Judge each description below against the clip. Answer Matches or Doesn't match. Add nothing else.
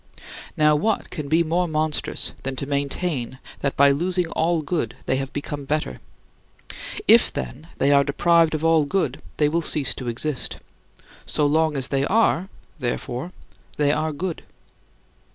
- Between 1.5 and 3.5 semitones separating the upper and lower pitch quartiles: Matches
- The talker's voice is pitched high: Doesn't match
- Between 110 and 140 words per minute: Doesn't match